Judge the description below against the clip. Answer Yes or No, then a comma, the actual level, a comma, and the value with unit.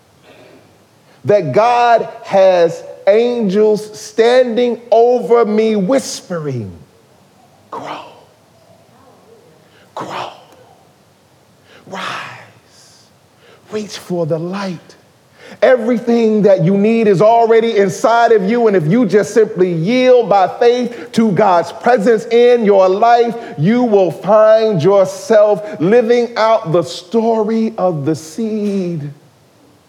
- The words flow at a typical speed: No, slow, 100 wpm